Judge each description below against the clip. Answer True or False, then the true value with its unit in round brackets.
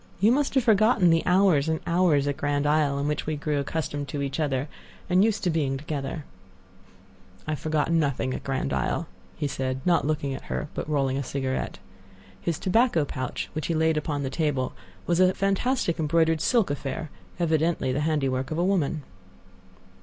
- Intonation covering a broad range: False (3.4 semitones)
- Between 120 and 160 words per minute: False (185 wpm)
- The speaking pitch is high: False (155 Hz)